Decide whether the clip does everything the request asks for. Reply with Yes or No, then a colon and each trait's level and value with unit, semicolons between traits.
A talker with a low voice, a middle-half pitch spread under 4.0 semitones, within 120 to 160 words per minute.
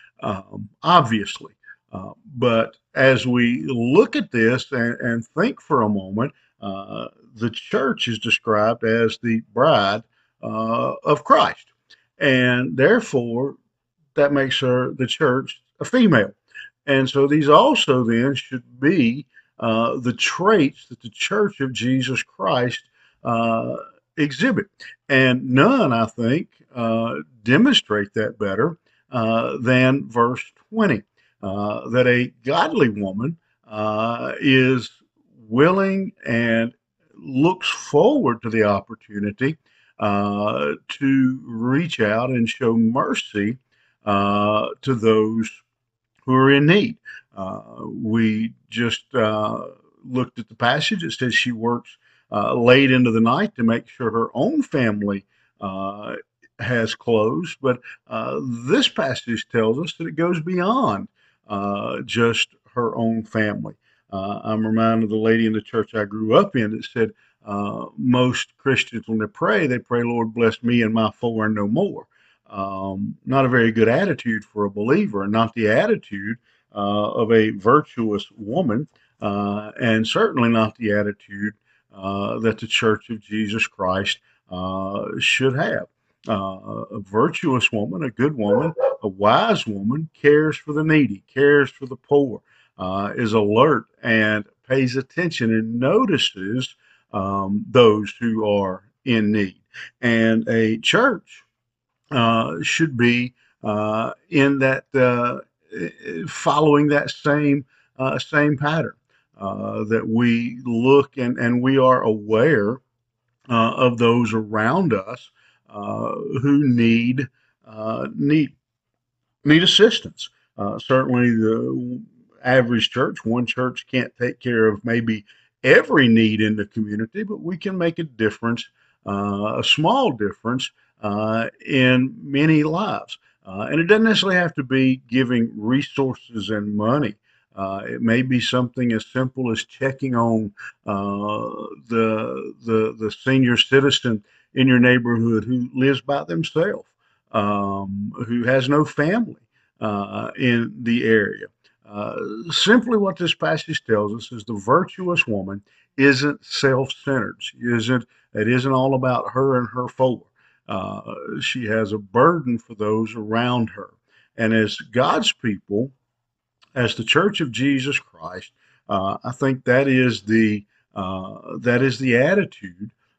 Yes: low, 120 Hz; average, 3.4 semitones; slow, 135 wpm